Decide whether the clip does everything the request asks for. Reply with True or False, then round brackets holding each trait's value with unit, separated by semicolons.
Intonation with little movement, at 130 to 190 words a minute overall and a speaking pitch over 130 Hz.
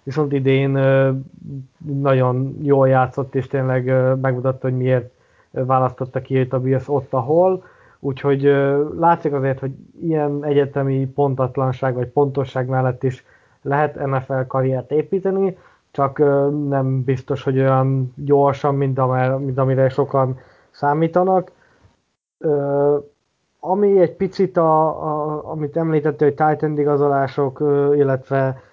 False (1.9 semitones; 110 wpm; 140 Hz)